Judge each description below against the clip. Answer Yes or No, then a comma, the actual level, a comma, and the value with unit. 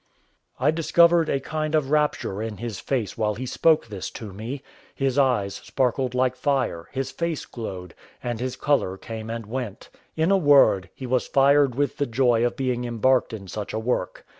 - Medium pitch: No, low, 125 Hz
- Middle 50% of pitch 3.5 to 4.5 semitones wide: Yes, average, 4.1 semitones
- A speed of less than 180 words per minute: No, average, 190 wpm